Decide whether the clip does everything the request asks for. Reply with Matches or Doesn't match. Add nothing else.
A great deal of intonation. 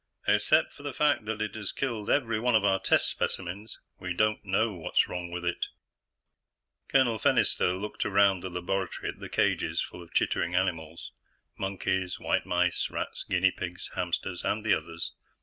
Doesn't match